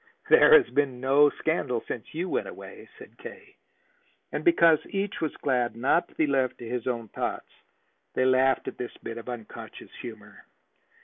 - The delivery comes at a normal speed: Yes, average, 175 wpm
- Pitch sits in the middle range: No, low, 130 Hz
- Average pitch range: Yes, average, 4.8 semitones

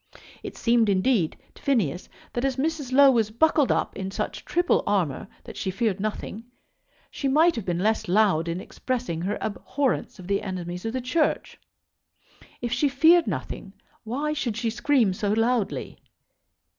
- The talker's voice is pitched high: Yes, high, 225 Hz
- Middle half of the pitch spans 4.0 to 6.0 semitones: Yes, wide, 5.6 semitones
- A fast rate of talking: No, average, 165 wpm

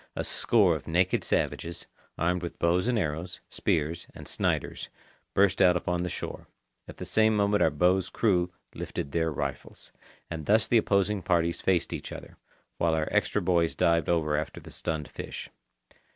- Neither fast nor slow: Yes, average, 170 wpm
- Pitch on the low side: Yes, very low, 85 Hz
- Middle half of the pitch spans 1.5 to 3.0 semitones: Yes, average, 2.7 semitones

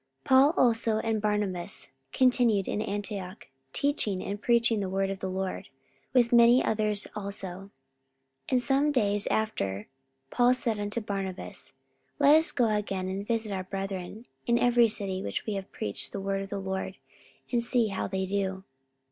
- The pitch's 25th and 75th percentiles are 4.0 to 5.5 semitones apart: No, average, 3.4 semitones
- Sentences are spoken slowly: No, average, 170 wpm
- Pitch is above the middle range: Yes, high, 205 Hz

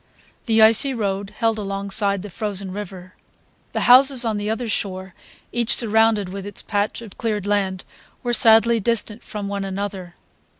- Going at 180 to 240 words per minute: No, average, 160 wpm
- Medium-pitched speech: No, high, 205 Hz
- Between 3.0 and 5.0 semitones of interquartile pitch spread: No, narrow, 2.4 semitones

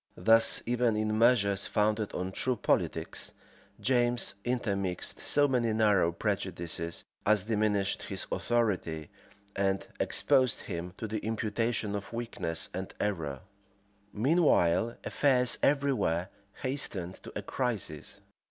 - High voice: No, low, 110 Hz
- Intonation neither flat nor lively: Yes, average, 4.2 semitones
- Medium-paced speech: No, slow, 125 wpm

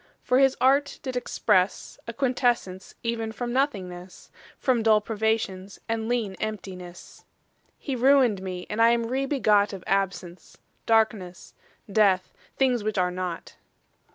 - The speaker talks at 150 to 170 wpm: No, slow, 135 wpm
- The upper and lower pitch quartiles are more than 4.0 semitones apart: Yes, average, 4.5 semitones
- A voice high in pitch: Yes, high, 220 Hz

